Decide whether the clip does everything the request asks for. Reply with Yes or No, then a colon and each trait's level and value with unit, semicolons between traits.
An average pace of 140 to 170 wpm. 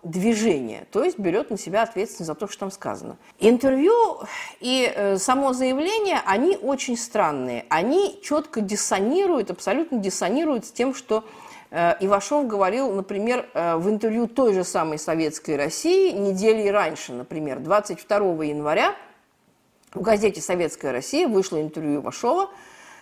No: average, 130 wpm